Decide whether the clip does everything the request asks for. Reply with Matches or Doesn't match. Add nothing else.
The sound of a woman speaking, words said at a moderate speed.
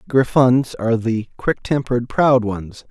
Doesn't match